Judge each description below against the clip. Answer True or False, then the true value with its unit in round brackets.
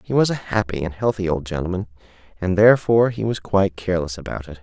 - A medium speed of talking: False (210 wpm)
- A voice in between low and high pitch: False (95 Hz)